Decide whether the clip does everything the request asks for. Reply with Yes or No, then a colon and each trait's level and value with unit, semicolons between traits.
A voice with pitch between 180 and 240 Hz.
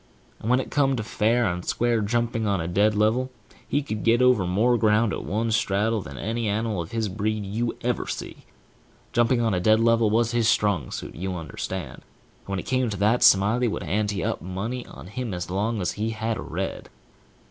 No: low, 110 Hz